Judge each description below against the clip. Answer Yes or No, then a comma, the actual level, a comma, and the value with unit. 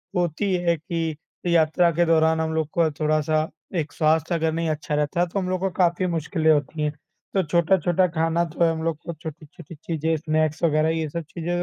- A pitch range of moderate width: No, narrow, 1.7 semitones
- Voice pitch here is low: No, medium, 160 Hz